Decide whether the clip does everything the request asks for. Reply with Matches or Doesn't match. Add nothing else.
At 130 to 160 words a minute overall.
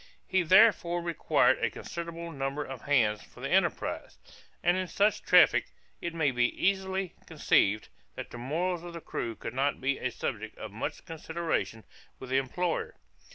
Doesn't match